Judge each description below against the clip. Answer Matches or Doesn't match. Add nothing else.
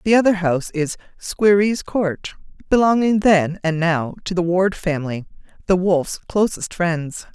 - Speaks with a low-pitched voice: Doesn't match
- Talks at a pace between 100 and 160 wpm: Matches